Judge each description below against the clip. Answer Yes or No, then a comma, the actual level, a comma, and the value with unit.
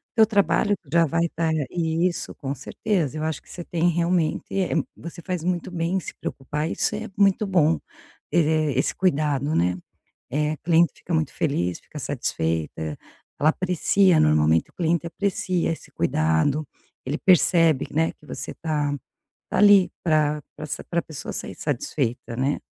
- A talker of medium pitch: Yes, medium, 160 Hz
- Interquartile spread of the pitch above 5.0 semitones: No, average, 3.5 semitones